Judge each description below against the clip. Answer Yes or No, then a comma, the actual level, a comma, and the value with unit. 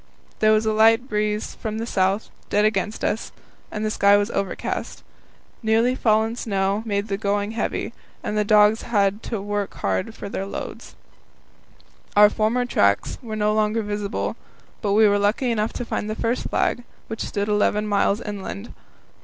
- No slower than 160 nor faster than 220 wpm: Yes, average, 170 wpm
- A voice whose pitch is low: No, high, 210 Hz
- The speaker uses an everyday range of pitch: No, narrow, 1.5 semitones